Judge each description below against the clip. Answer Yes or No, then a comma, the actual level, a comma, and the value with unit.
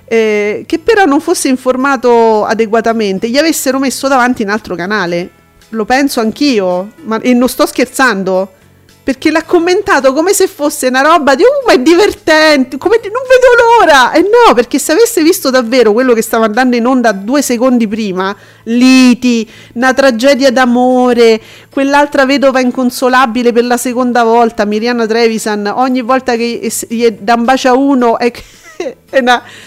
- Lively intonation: No, average, 3.7 semitones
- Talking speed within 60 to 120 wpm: No, fast, 170 wpm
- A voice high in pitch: Yes, very high, 255 Hz